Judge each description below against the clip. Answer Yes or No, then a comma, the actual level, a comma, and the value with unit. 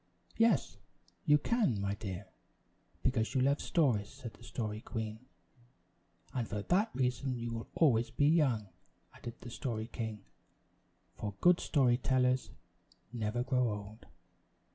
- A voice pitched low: Yes, low, 120 Hz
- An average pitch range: Yes, average, 3.6 semitones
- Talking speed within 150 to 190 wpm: No, slow, 135 wpm